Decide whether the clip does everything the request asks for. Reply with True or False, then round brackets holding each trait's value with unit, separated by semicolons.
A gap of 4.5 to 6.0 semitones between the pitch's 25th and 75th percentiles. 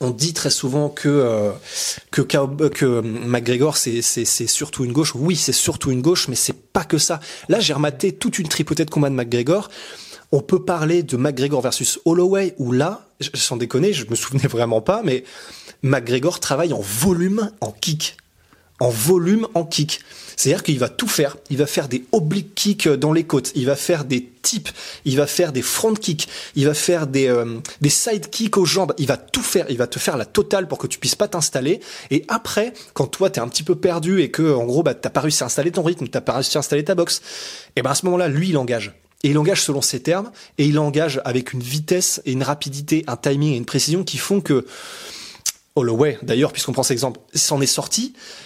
True (4.9 semitones)